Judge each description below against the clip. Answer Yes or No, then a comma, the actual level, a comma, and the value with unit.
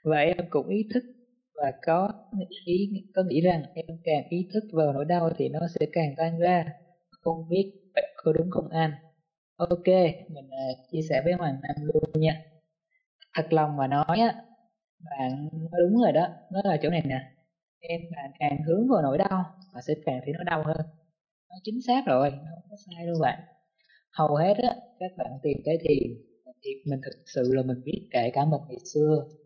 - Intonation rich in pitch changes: No, average, 3.7 semitones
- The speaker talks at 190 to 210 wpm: Yes, average, 200 wpm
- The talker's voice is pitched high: No, medium, 165 Hz